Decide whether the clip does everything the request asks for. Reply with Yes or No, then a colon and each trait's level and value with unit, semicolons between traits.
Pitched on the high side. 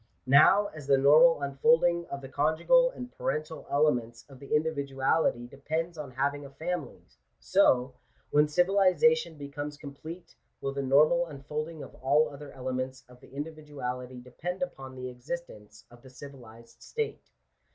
No: medium, 145 Hz